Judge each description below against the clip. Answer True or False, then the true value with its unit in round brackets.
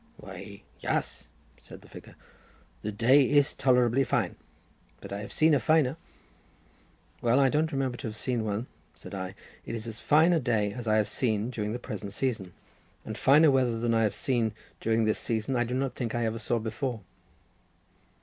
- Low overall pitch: True (120 Hz)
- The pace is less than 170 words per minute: False (190 wpm)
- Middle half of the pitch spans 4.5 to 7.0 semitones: False (3.4 semitones)